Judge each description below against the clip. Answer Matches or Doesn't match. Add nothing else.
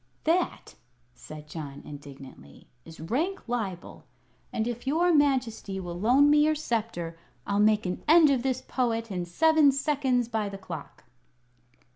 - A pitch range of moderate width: Doesn't match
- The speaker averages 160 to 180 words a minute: Doesn't match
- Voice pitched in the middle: Doesn't match